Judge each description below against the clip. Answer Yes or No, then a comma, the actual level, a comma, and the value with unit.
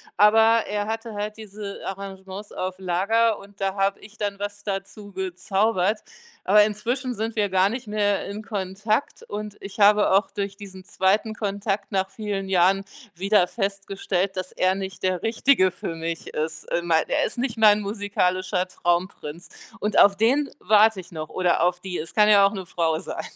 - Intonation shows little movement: Yes, narrow, 2.2 semitones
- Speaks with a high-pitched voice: Yes, high, 200 Hz